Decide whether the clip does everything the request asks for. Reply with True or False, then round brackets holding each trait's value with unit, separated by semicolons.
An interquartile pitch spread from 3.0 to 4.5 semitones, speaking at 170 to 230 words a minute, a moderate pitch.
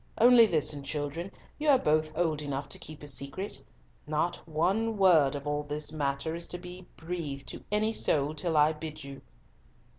True (3.4 semitones; 180 wpm; 155 Hz)